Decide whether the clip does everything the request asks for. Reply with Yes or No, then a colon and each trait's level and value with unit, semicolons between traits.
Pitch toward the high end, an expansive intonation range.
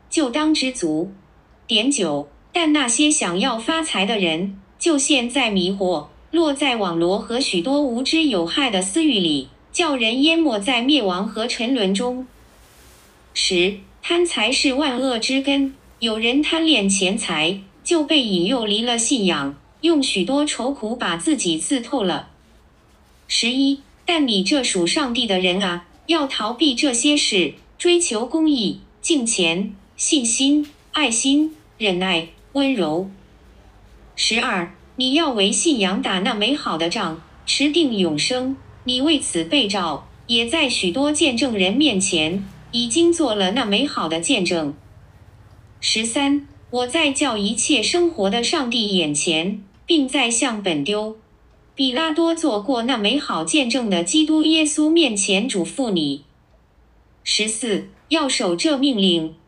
Yes: high, 235 Hz; wide, 7.8 semitones